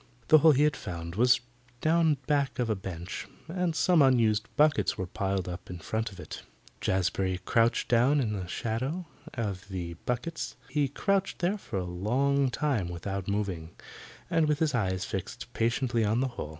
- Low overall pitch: Yes, low, 115 Hz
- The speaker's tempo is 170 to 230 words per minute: Yes, average, 175 wpm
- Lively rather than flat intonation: Yes, wide, 7.1 semitones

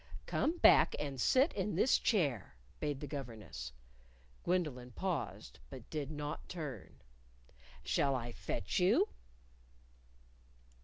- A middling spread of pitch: No, wide, 6.2 semitones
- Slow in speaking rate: Yes, slow, 110 wpm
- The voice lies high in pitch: No, medium, 145 Hz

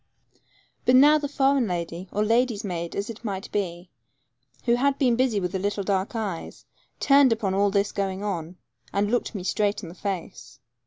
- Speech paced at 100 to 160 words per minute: No, average, 180 wpm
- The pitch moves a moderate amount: Yes, average, 4.2 semitones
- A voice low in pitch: No, high, 205 Hz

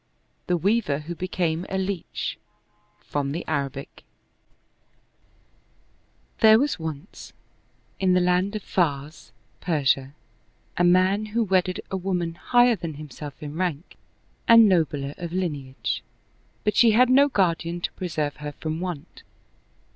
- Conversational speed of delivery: No, slow, 130 wpm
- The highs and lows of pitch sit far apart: No, average, 4.3 semitones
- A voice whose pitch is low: No, medium, 175 Hz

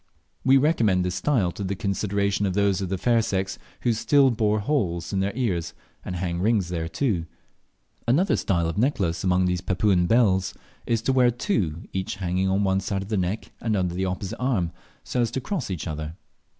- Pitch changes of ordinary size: Yes, average, 4.1 semitones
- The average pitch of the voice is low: Yes, very low, 95 Hz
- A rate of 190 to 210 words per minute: Yes, average, 200 wpm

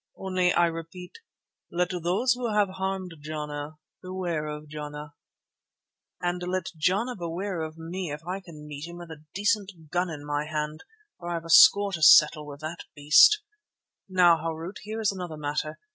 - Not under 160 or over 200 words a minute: Yes, average, 170 wpm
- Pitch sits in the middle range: Yes, medium, 170 Hz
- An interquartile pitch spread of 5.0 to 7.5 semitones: No, average, 3.5 semitones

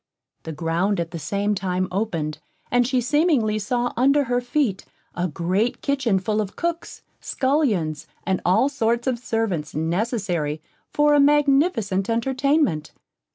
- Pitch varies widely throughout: Yes, wide, 6.6 semitones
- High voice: Yes, high, 220 Hz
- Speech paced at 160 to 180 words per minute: No, average, 140 wpm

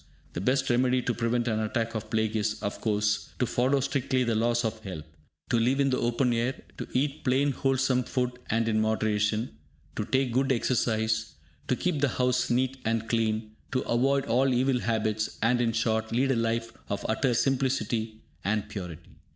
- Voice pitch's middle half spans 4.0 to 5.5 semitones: No, average, 2.7 semitones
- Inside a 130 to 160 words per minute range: No, average, 185 wpm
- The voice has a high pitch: No, low, 120 Hz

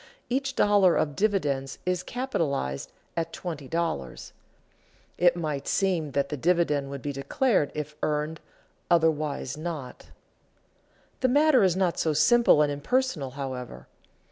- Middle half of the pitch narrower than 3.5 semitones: No, average, 4.8 semitones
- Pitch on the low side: No, medium, 160 Hz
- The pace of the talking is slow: Yes, slow, 125 wpm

